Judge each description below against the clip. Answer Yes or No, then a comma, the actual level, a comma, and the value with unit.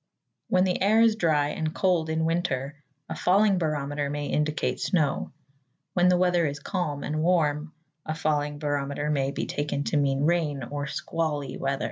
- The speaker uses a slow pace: No, average, 170 wpm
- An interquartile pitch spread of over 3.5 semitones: No, average, 3.2 semitones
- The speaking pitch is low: No, medium, 150 Hz